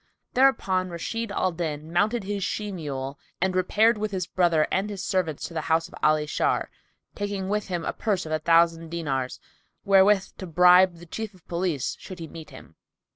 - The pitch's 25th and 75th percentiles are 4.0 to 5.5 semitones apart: No, average, 3.4 semitones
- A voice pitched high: No, medium, 180 Hz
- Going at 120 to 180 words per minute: No, average, 190 wpm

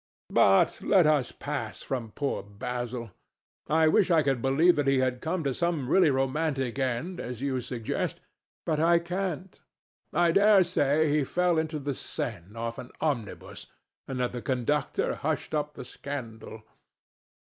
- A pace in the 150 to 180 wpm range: Yes, average, 160 wpm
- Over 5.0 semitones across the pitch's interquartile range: No, average, 4.5 semitones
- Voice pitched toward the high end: No, medium, 140 Hz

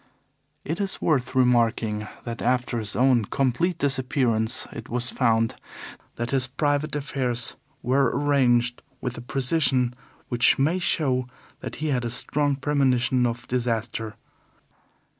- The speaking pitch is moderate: No, low, 125 Hz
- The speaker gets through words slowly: Yes, slow, 130 wpm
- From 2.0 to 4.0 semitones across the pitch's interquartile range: Yes, average, 2.7 semitones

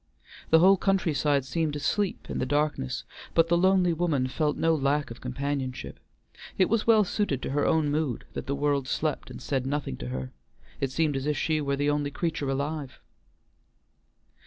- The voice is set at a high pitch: No, medium, 145 Hz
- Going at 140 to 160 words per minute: No, average, 185 wpm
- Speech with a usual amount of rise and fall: Yes, average, 3.0 semitones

